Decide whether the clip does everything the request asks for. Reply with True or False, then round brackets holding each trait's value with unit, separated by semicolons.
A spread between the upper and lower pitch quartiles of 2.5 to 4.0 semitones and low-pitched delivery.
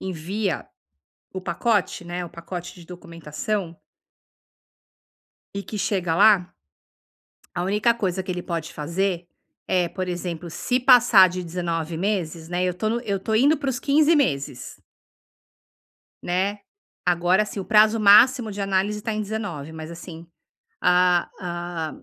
False (3.5 semitones; 185 Hz)